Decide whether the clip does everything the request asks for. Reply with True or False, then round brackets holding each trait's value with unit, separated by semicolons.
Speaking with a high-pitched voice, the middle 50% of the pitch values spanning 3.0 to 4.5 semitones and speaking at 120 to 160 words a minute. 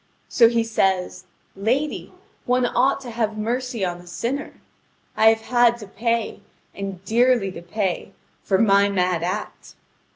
True (220 Hz; 3.8 semitones; 150 wpm)